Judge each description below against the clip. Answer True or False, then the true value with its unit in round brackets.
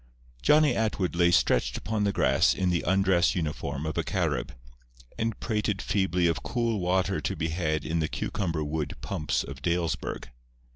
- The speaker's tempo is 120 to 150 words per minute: False (165 wpm)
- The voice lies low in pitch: True (90 Hz)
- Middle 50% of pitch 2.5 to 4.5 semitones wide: True (3.9 semitones)